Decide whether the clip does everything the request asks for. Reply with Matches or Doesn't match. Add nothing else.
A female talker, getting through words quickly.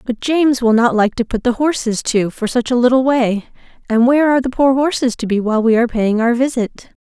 Matches